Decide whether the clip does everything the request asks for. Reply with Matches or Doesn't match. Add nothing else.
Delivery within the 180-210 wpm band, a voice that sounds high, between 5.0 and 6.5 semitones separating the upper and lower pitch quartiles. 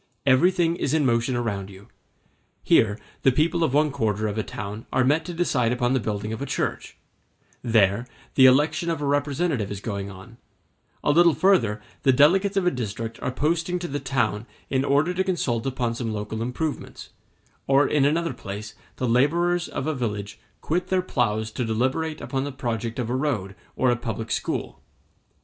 Doesn't match